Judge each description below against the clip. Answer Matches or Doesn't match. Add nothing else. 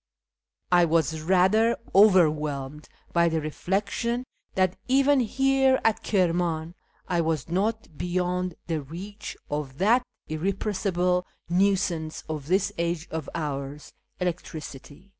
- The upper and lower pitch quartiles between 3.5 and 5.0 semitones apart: Matches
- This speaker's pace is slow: Matches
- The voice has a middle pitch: Matches